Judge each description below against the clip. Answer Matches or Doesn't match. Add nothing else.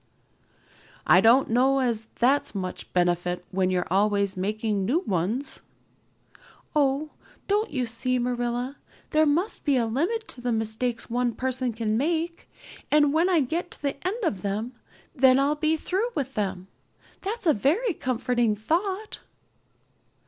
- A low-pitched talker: Doesn't match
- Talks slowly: Doesn't match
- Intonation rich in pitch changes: Matches